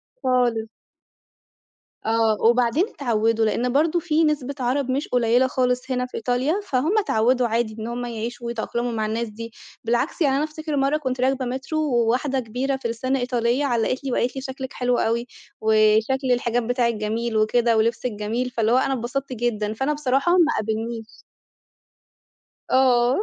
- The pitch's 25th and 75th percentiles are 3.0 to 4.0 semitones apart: No, narrow, 2.6 semitones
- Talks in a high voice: Yes, high, 245 Hz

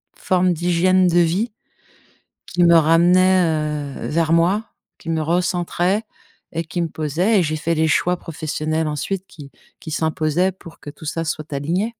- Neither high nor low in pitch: Yes, medium, 170 Hz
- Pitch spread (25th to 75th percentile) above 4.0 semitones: No, narrow, 2.5 semitones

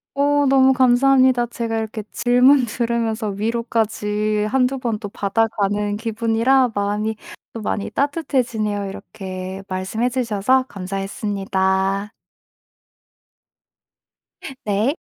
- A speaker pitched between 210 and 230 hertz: Yes, high, 220 Hz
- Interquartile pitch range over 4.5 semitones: No, average, 3.5 semitones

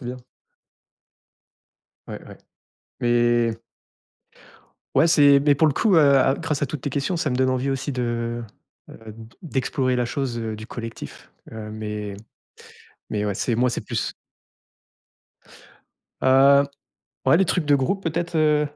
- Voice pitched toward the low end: Yes, low, 130 Hz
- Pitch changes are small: No, average, 3.7 semitones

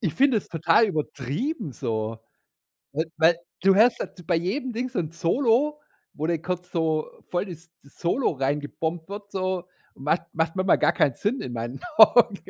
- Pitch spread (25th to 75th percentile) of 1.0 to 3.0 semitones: No, average, 5.1 semitones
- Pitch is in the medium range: Yes, medium, 170 Hz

